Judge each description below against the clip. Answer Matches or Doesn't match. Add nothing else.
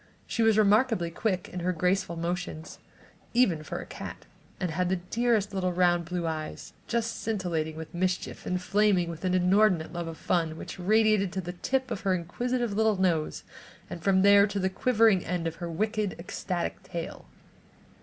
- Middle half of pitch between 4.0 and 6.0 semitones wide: Doesn't match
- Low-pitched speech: Doesn't match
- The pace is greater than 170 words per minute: Matches